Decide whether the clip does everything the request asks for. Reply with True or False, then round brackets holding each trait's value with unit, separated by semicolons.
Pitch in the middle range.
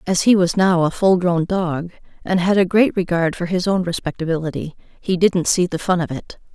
True (180 Hz)